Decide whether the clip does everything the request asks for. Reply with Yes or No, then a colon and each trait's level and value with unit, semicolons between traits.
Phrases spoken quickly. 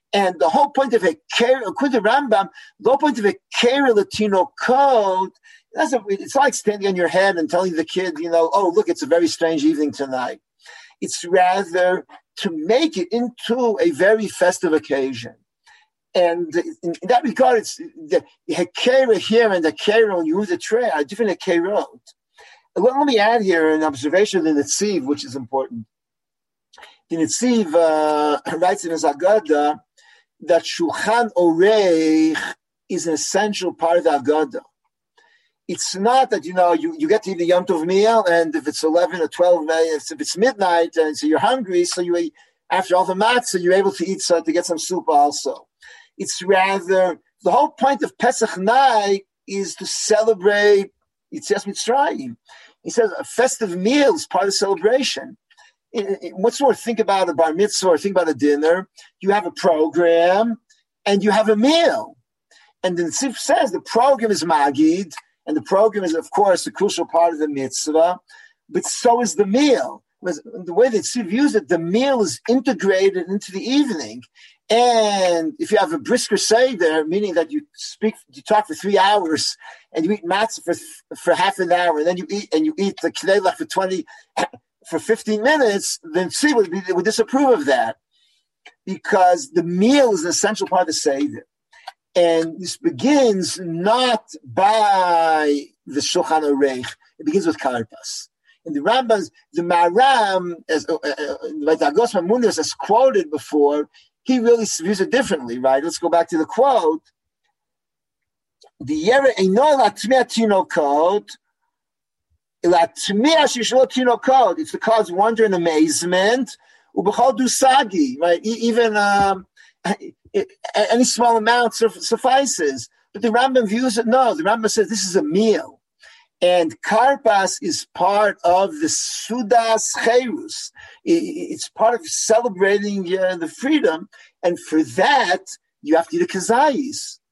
No: average, 165 wpm